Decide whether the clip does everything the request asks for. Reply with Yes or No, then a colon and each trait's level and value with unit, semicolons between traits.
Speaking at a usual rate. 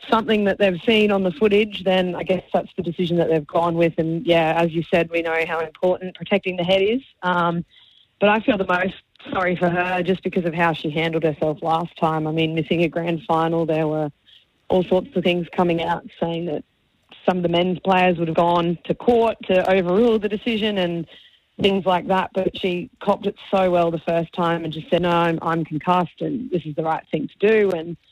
No: fast, 230 wpm